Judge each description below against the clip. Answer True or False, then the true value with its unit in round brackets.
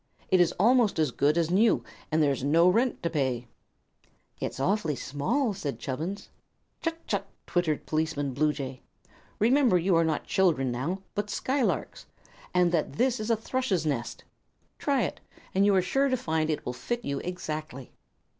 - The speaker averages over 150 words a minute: True (170 wpm)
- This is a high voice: False (170 Hz)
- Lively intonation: True (6.0 semitones)